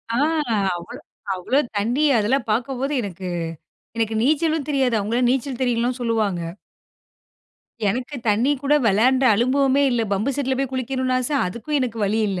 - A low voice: No, high, 245 Hz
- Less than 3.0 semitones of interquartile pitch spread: No, average, 3.5 semitones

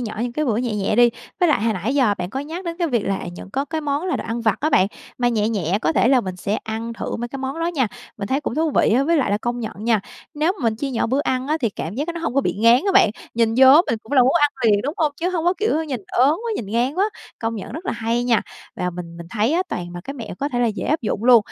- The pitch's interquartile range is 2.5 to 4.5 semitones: No, average, 5.1 semitones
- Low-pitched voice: No, high, 245 Hz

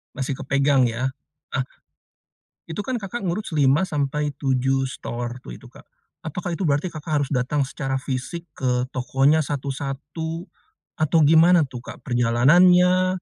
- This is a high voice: No, medium, 140 Hz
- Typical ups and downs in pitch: Yes, average, 3.9 semitones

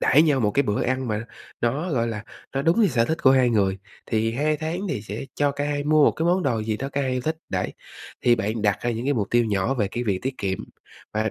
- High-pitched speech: No, low, 125 Hz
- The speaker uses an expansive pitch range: No, average, 4.7 semitones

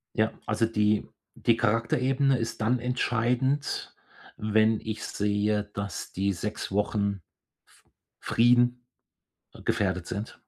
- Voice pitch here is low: Yes, low, 110 Hz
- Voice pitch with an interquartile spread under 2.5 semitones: No, average, 2.8 semitones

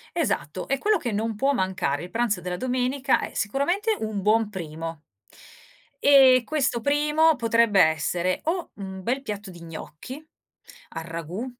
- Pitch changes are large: Yes, wide, 7.1 semitones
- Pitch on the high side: Yes, high, 225 Hz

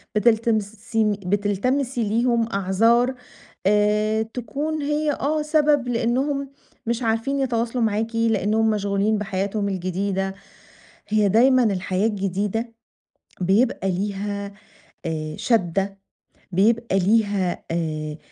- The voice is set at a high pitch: Yes, high, 215 Hz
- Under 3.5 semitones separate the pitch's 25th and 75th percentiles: Yes, average, 3.1 semitones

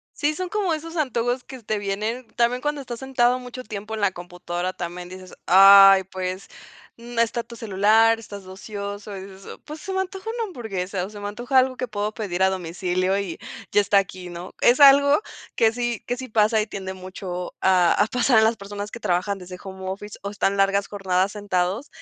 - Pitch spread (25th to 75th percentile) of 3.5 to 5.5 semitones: Yes, average, 4.3 semitones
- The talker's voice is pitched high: Yes, high, 205 Hz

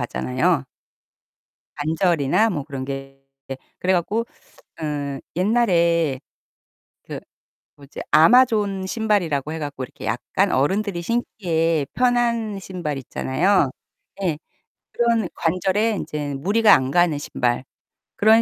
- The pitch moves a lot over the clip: Yes, wide, 6.4 semitones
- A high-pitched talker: No, medium, 170 Hz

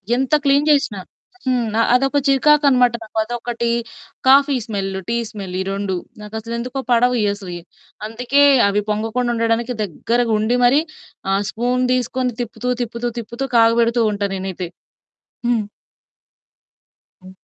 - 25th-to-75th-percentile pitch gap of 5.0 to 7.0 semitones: No, average, 3.0 semitones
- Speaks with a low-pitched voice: No, high, 235 Hz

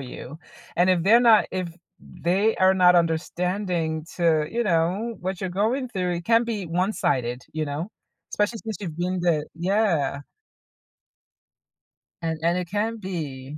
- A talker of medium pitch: Yes, medium, 180 Hz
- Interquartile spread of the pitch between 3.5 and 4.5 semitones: Yes, average, 4.0 semitones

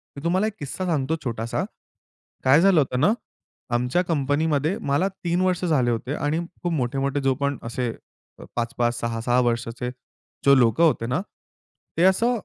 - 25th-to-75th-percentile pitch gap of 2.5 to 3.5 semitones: No, wide, 5.5 semitones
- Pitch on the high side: No, medium, 140 Hz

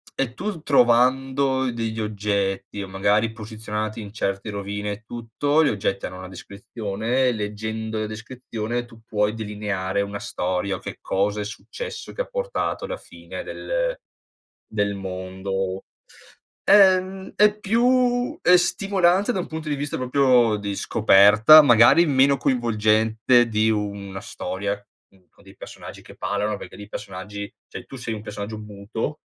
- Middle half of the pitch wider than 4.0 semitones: Yes, average, 4.8 semitones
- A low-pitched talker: Yes, low, 110 Hz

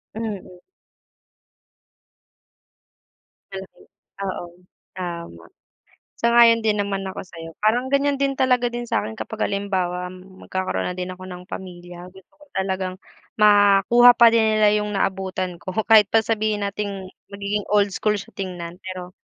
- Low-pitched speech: No, high, 195 Hz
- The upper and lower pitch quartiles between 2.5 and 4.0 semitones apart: Yes, average, 3.0 semitones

